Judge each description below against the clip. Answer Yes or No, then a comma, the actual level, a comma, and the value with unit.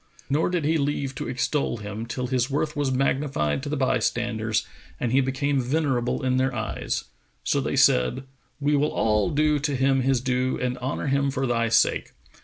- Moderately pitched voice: No, low, 130 Hz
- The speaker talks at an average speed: Yes, average, 185 wpm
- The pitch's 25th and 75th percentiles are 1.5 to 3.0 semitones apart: Yes, average, 2.7 semitones